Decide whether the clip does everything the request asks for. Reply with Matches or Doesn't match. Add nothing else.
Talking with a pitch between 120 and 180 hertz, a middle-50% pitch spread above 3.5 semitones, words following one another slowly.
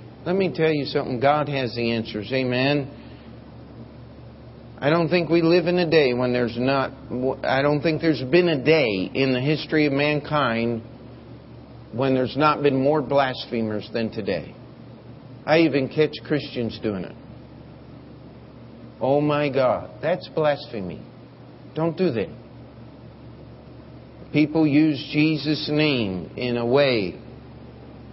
Matches